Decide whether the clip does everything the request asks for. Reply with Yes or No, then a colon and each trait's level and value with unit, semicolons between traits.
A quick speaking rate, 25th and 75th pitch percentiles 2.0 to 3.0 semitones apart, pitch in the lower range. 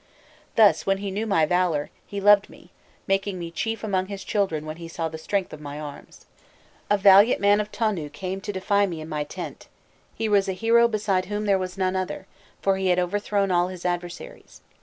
No: fast, 210 wpm; narrow, 2.6 semitones; high, 190 Hz